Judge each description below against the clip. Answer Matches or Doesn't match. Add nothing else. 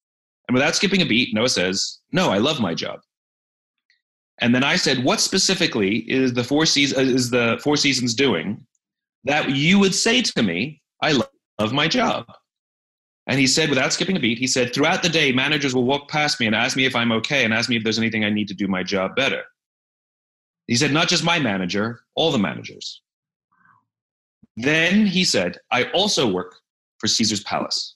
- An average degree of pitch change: Doesn't match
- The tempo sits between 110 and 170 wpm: Doesn't match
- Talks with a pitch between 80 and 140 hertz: Matches